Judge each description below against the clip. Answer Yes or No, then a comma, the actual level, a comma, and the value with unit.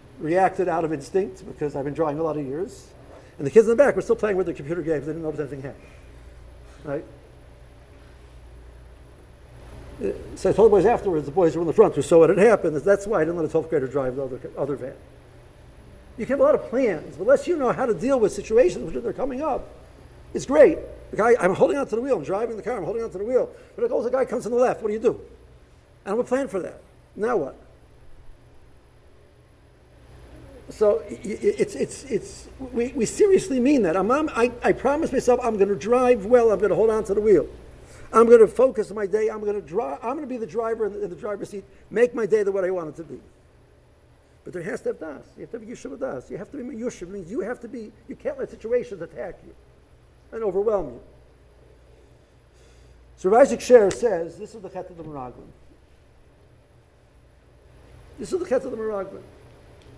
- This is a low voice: No, high, 215 Hz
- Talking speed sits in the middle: No, fast, 220 wpm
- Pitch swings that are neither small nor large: No, wide, 8.3 semitones